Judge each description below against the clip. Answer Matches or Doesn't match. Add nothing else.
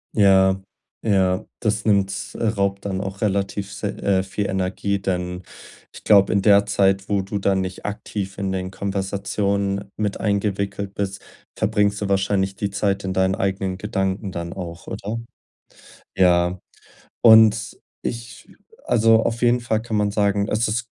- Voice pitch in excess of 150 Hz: Doesn't match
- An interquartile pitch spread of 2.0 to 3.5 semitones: Doesn't match